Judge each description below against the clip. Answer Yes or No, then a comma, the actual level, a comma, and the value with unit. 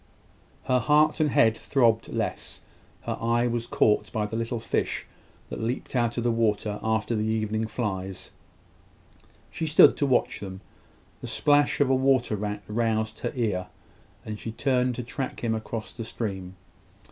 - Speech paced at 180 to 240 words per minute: No, average, 165 wpm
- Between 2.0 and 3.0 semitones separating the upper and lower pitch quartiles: Yes, narrow, 2.6 semitones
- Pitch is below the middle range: Yes, low, 115 Hz